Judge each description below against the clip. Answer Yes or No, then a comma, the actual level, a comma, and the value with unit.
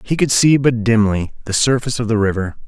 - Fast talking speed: Yes, fast, 225 wpm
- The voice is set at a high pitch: No, low, 115 Hz